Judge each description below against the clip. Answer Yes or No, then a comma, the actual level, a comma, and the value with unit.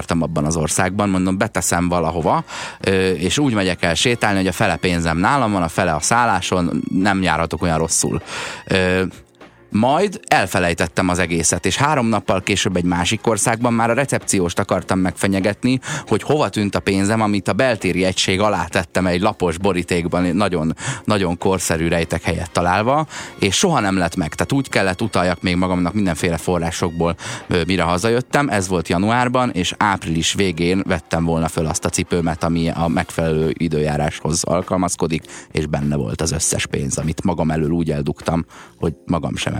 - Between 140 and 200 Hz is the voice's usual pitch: No, very low, 95 Hz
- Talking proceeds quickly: Yes, fast, 165 wpm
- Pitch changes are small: No, average, 3.1 semitones